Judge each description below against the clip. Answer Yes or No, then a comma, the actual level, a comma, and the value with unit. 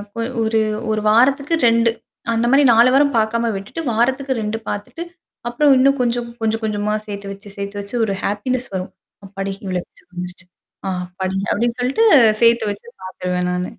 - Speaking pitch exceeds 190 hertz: Yes, high, 220 Hz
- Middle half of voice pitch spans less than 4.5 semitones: Yes, average, 3.7 semitones